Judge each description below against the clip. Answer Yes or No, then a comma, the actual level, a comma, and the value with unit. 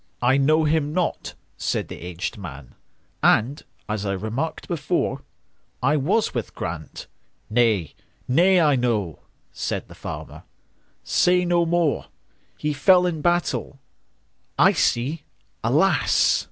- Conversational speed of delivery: No, slow, 100 wpm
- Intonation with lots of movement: Yes, wide, 7.5 semitones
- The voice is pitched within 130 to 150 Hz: Yes, medium, 140 Hz